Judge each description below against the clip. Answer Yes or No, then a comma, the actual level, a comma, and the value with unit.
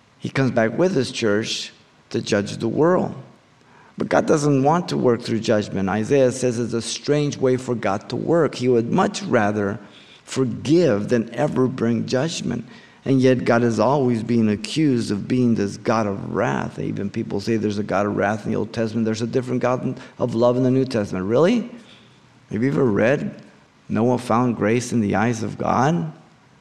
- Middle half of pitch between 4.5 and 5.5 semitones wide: No, average, 3.2 semitones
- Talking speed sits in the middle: Yes, average, 190 wpm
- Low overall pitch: Yes, low, 120 Hz